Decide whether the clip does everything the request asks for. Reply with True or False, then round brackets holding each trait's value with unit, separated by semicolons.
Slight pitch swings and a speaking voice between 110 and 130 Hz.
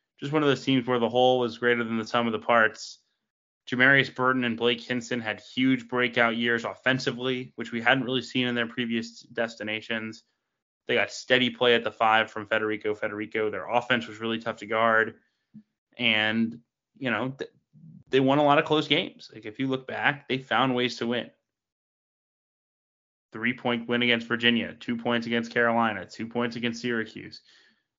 True (1.9 semitones; 120 Hz)